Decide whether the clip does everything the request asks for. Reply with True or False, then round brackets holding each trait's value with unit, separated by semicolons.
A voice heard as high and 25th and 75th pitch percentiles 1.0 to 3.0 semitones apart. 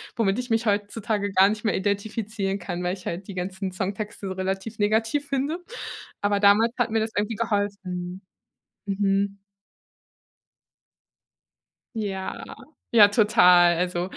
True (200 Hz; 2.5 semitones)